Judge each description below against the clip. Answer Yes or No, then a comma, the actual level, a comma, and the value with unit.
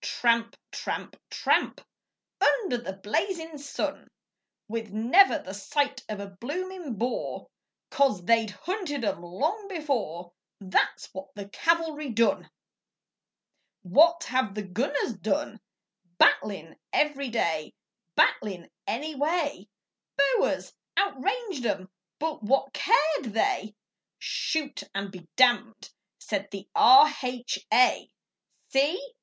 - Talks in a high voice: Yes, very high, 255 Hz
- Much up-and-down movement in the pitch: Yes, wide, 6.7 semitones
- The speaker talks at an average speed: No, slow, 105 wpm